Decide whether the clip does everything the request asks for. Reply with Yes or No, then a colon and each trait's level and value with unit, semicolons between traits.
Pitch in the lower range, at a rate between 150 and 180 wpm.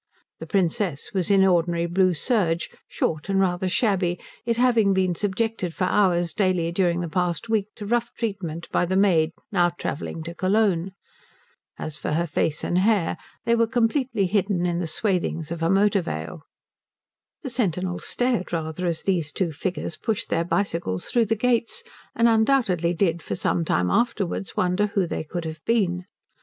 No: medium, 185 Hz; average, 175 wpm